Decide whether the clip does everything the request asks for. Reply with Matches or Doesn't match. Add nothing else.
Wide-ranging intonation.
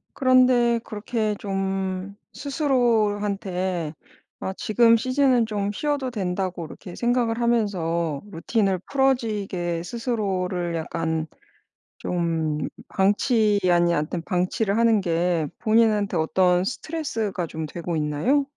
Doesn't match